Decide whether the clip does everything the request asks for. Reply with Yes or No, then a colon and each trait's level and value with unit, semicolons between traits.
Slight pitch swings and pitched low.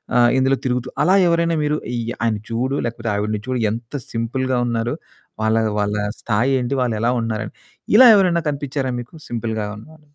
No: average, 3.2 semitones; low, 120 Hz